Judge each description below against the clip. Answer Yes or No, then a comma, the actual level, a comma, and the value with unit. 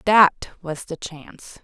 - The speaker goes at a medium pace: Yes, average, 145 wpm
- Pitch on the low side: No, medium, 175 Hz